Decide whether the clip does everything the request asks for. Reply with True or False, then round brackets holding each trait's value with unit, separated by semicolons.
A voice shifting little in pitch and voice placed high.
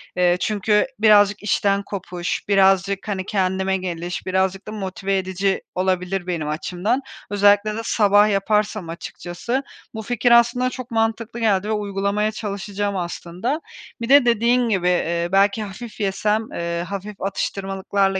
True (2.3 semitones; 200 Hz)